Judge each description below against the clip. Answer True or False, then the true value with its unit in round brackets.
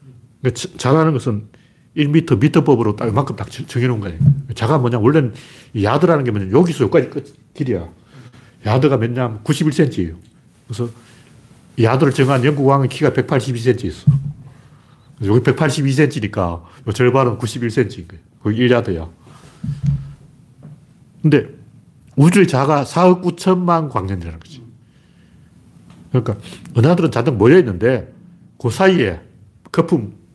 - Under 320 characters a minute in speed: True (265 characters per minute)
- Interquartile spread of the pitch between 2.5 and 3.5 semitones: False (4.2 semitones)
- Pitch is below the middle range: True (130 Hz)